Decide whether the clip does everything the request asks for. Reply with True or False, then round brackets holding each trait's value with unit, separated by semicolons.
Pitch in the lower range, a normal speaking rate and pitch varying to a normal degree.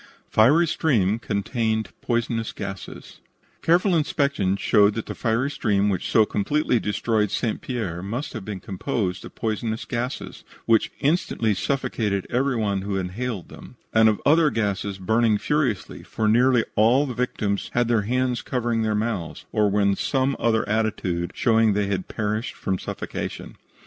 True (110 Hz; 160 wpm; 3.5 semitones)